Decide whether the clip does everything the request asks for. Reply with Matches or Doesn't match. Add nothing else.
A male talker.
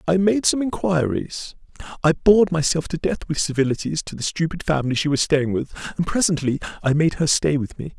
Matches